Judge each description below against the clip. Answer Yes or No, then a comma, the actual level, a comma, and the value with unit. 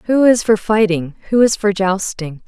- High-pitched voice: Yes, high, 200 Hz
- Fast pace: No, average, 195 wpm